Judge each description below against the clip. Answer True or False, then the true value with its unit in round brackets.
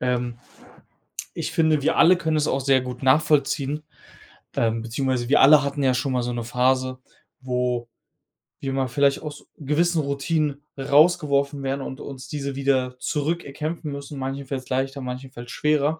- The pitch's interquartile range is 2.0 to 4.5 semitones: True (2.5 semitones)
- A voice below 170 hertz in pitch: True (140 Hz)